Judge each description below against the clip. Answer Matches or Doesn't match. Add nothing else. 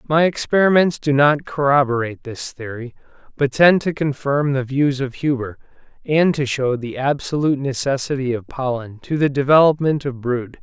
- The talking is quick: Doesn't match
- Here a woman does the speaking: Doesn't match